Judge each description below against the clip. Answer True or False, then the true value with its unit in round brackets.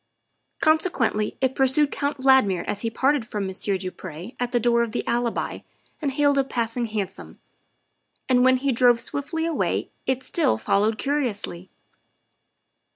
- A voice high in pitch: True (245 Hz)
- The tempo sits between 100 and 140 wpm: False (155 wpm)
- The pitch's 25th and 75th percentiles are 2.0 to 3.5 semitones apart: False (4.4 semitones)